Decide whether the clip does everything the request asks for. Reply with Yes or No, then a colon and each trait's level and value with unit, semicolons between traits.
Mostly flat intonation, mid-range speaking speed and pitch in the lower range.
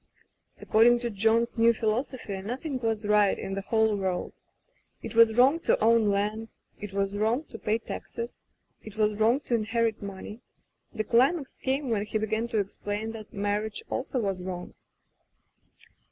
No: narrow, 2.2 semitones; average, 165 wpm; high, 220 Hz